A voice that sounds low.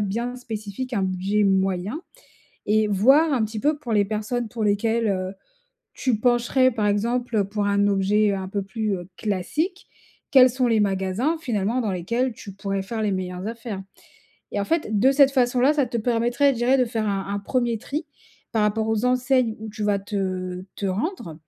No: high, 215 Hz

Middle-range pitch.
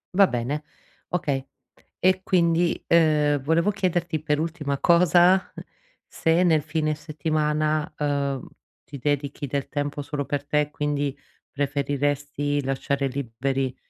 Yes: medium, 150 Hz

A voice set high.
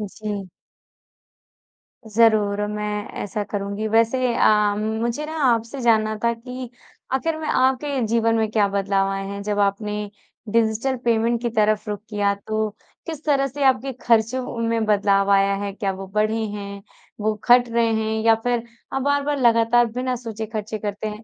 Yes: high, 220 Hz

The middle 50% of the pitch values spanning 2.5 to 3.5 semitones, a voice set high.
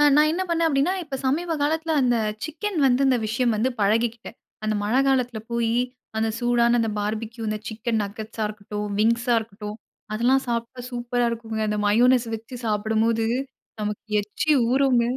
Yes: average, 2.9 semitones; high, 235 Hz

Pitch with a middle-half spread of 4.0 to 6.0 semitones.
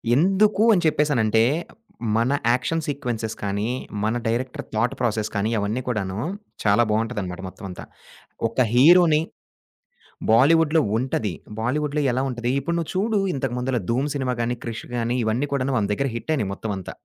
Yes: average, 4.9 semitones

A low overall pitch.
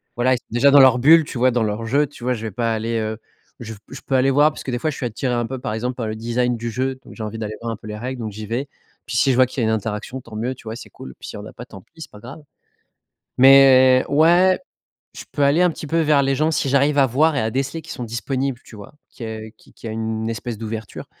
Yes: low, 125 Hz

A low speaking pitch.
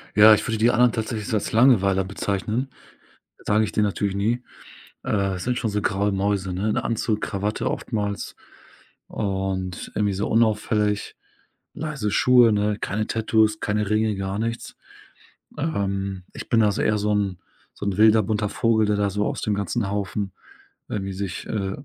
Yes: low, 105 Hz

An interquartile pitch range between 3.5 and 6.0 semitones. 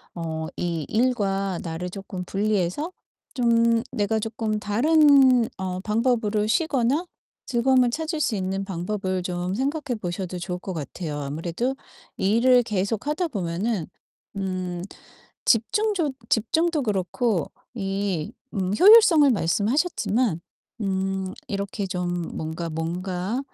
Yes: average, 5.3 semitones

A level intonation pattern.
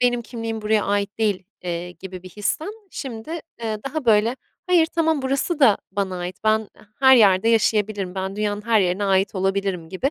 No: average, 3.7 semitones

